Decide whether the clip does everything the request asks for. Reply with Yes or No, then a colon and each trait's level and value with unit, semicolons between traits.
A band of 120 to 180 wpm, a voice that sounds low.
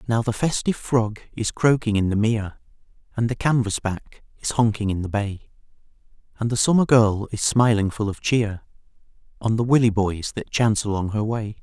Yes: average, 175 wpm; low, 110 Hz